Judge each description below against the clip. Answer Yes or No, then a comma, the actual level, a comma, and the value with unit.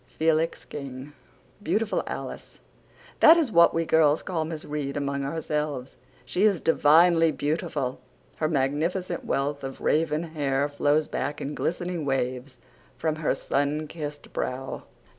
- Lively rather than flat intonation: No, average, 2.7 semitones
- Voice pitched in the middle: Yes, medium, 150 Hz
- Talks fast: No, slow, 135 wpm